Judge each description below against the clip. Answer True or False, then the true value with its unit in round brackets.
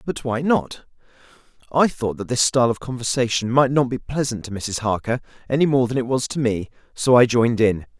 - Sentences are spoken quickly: True (210 wpm)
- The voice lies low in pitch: True (125 Hz)